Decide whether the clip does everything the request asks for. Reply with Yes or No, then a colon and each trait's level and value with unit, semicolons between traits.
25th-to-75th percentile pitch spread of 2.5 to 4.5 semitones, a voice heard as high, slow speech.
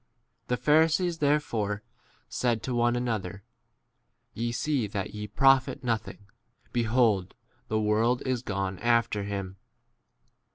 No: average, 3.4 semitones; low, 115 Hz; slow, 115 wpm